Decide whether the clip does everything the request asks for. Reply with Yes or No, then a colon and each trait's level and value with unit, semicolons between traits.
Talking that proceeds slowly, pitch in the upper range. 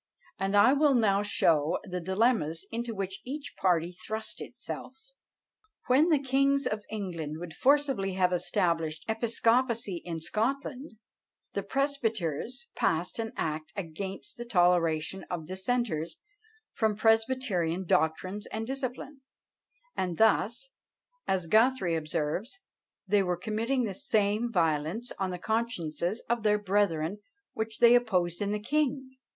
Yes: slow, 130 wpm; high, 205 Hz